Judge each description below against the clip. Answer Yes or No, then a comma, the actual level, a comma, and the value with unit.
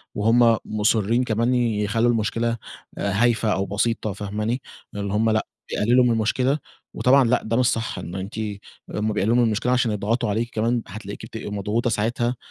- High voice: No, low, 115 Hz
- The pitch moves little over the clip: Yes, narrow, 2.3 semitones